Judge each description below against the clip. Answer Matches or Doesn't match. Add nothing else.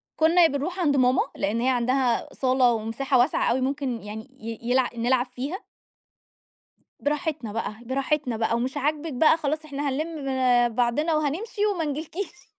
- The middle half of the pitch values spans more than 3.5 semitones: Matches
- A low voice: Doesn't match